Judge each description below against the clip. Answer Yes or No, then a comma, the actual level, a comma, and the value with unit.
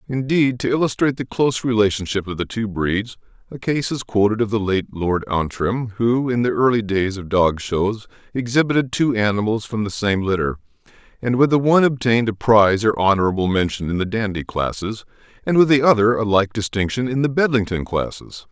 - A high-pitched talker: No, low, 110 Hz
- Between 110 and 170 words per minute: No, average, 190 wpm